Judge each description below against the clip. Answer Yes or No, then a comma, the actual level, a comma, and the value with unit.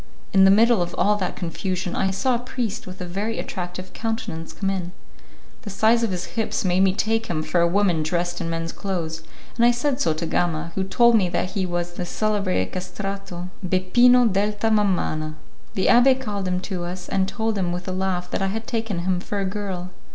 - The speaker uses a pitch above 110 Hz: Yes, high, 190 Hz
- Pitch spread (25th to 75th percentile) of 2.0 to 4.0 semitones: Yes, average, 3.3 semitones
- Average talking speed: No, fast, 215 wpm